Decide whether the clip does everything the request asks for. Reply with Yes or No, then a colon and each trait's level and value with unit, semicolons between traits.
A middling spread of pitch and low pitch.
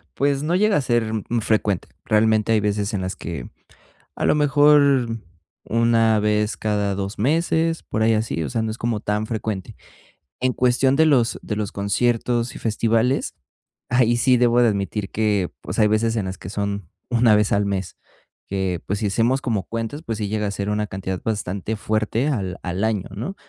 Yes: average, 3.0 semitones; low, 110 Hz